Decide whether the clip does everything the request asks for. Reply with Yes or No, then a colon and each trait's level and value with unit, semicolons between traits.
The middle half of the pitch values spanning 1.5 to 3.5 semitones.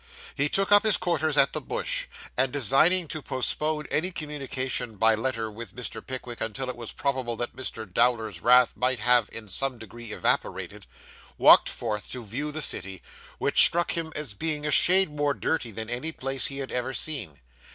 No: average, 4.4 semitones